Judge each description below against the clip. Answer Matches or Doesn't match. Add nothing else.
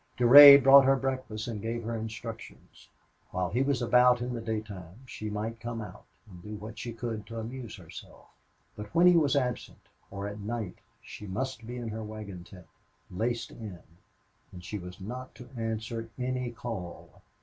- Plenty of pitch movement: Doesn't match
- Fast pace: Doesn't match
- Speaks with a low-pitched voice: Matches